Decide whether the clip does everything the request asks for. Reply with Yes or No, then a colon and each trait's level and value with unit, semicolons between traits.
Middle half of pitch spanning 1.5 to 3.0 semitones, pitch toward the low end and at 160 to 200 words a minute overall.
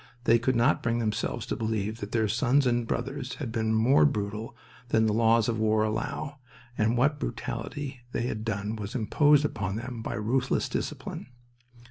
Yes: average, 2.7 semitones; low, 115 Hz; average, 175 wpm